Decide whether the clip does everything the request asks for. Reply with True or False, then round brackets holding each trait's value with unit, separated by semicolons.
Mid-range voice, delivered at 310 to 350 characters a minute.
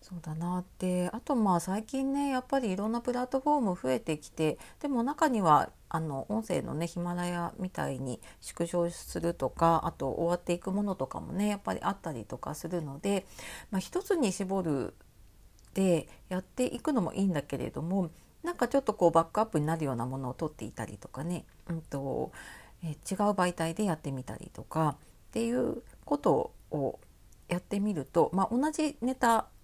False (180 Hz; 365 characters per minute)